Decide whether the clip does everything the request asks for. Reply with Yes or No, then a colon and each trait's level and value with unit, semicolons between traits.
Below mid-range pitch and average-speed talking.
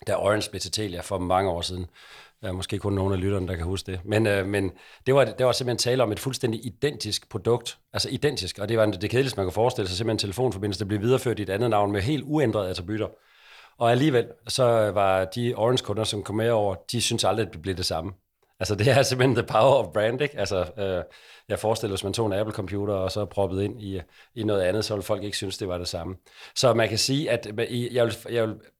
No: low, 105 Hz; fast, 250 wpm